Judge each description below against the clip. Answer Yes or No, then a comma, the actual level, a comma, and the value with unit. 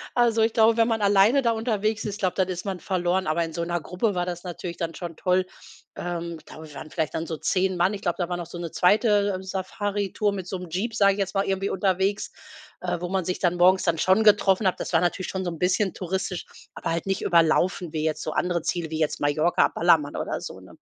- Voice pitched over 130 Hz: Yes, medium, 185 Hz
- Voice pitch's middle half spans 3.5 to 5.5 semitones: No, narrow, 2.6 semitones